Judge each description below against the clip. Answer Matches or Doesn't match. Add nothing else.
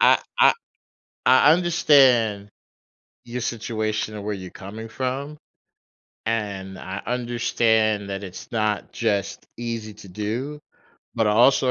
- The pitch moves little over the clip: Doesn't match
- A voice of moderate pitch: Doesn't match